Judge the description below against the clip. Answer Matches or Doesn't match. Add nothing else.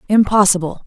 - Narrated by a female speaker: Matches